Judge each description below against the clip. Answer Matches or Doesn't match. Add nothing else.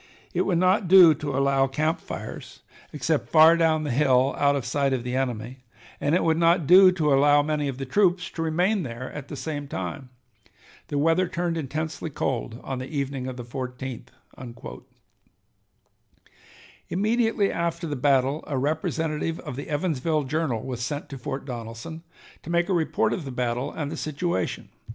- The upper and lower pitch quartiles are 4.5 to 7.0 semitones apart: Doesn't match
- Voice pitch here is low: Doesn't match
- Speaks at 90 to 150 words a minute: Doesn't match